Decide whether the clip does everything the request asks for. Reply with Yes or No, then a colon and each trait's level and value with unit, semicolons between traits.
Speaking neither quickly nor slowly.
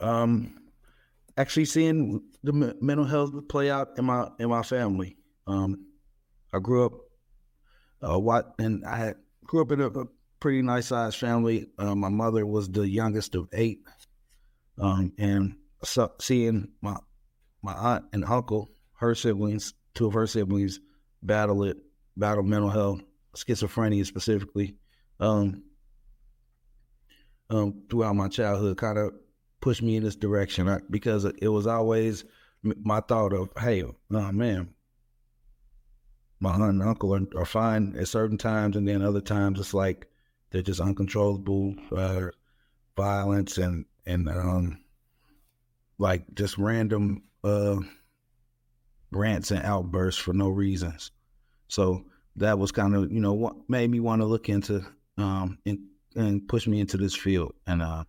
Yes: average, 150 wpm